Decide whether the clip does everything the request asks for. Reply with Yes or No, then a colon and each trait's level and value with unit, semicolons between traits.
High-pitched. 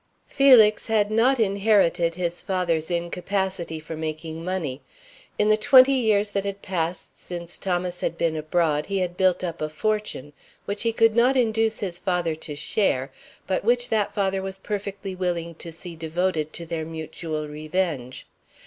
No: medium, 180 Hz